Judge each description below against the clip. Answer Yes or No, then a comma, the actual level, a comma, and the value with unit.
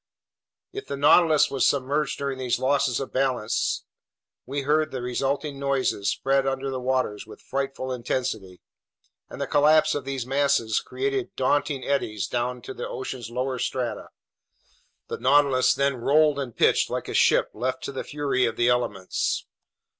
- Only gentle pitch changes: Yes, narrow, 2.2 semitones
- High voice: No, low, 135 Hz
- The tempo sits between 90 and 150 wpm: No, average, 160 wpm